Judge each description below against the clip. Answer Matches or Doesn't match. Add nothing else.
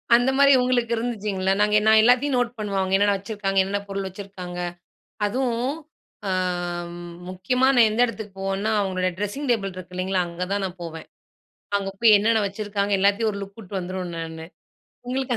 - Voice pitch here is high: Matches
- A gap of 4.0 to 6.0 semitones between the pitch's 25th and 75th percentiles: Doesn't match